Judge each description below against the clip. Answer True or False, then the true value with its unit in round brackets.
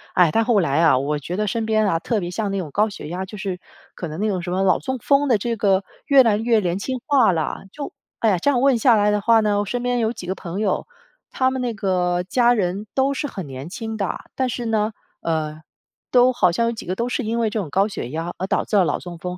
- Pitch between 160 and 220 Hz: True (205 Hz)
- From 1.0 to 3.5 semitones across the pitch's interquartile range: False (4.7 semitones)